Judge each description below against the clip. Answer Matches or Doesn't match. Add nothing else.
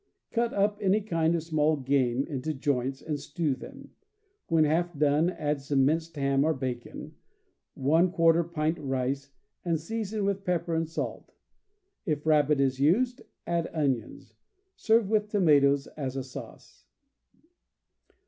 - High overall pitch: Doesn't match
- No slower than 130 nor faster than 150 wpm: Matches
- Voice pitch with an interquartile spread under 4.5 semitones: Matches